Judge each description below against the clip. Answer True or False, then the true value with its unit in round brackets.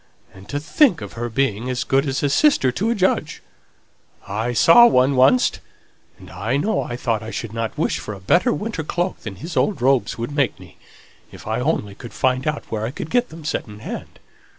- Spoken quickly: True (215 wpm)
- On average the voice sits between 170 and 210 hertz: False (130 Hz)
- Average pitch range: False (6.0 semitones)